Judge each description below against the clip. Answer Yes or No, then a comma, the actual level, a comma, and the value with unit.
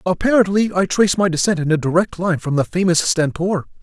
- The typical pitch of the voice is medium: Yes, medium, 175 Hz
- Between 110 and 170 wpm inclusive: No, fast, 205 wpm